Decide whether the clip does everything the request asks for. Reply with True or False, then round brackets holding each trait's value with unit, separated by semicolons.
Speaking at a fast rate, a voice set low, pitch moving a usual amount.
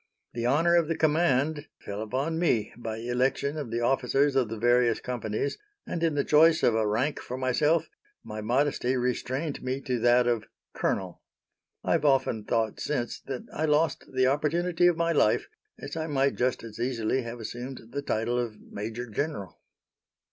False (175 wpm; 130 Hz; 4.2 semitones)